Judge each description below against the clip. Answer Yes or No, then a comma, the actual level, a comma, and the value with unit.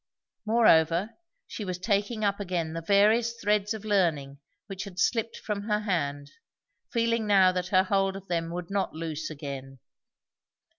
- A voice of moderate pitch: No, high, 195 Hz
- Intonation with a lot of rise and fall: No, average, 4.0 semitones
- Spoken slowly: No, average, 155 wpm